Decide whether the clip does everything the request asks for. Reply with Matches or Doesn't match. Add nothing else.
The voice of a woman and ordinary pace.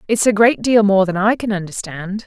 Doesn't match